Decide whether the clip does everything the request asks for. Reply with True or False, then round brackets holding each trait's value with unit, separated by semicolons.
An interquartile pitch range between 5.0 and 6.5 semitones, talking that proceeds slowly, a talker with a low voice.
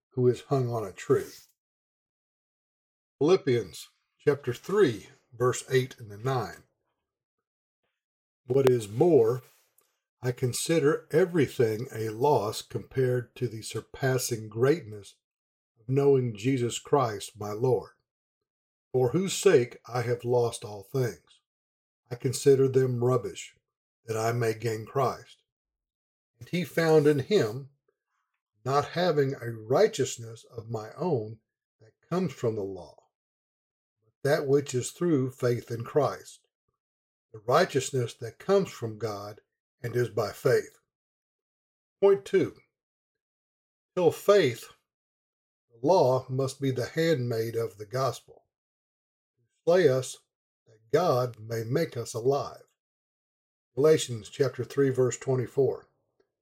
False (3.7 semitones; 120 wpm; 125 Hz)